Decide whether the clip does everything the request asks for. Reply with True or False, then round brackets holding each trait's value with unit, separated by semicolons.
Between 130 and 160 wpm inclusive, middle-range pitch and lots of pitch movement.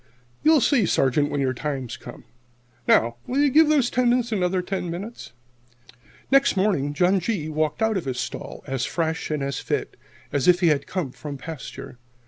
False (175 wpm; 170 Hz; 7.6 semitones)